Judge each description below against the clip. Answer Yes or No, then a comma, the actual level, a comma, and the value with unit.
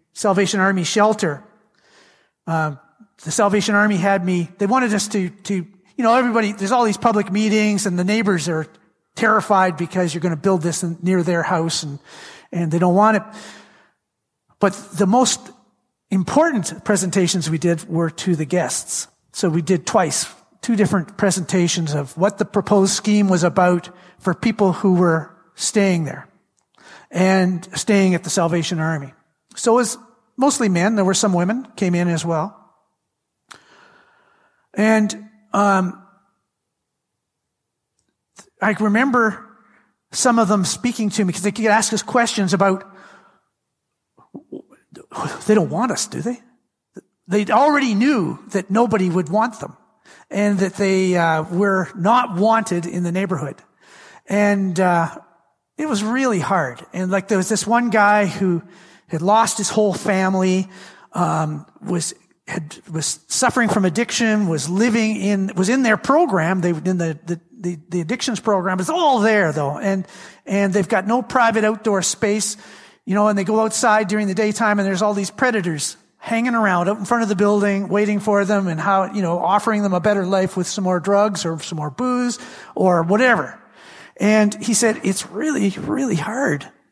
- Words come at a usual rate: Yes, average, 165 wpm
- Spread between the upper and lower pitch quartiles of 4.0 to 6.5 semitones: No, average, 3.3 semitones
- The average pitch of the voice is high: Yes, high, 200 Hz